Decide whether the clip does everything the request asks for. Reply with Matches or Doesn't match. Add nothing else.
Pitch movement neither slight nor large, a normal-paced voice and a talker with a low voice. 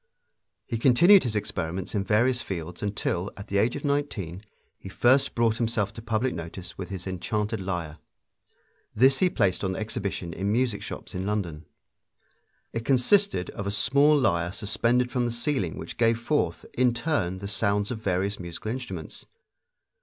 Matches